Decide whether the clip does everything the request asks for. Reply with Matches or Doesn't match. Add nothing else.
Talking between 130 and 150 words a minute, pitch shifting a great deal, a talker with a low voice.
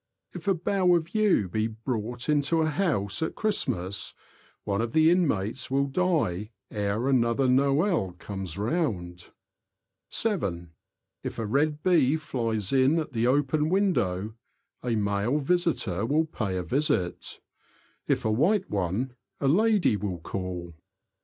Matches